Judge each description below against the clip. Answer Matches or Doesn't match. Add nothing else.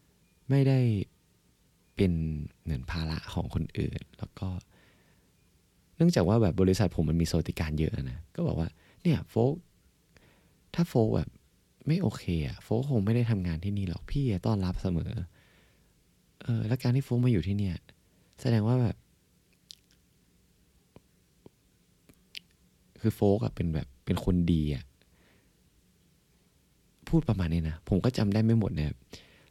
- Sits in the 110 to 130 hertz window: Doesn't match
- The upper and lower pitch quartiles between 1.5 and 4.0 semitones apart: Doesn't match